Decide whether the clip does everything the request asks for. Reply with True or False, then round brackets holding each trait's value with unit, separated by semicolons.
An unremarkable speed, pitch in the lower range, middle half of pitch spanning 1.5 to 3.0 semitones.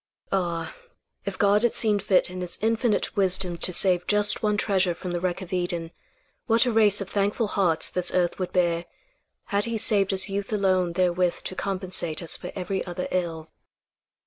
False (185 wpm; 185 Hz; 2.5 semitones)